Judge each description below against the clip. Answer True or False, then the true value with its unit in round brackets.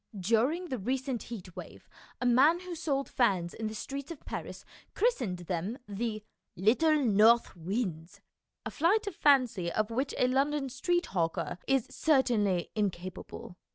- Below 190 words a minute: True (155 wpm)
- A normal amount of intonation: False (6.2 semitones)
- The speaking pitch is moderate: False (240 Hz)